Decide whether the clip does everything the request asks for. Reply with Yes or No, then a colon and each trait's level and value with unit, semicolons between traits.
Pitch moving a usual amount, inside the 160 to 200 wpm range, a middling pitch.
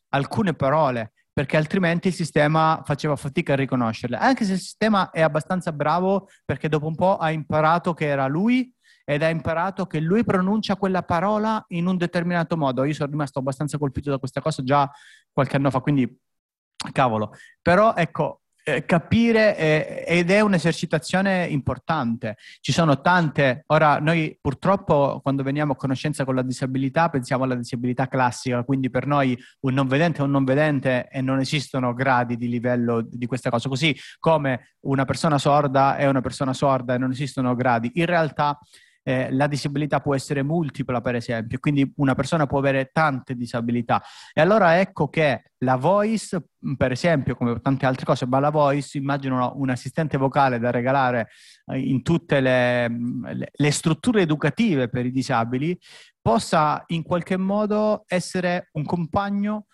Yes: average, 4.2 semitones; average, 165 wpm; medium, 145 Hz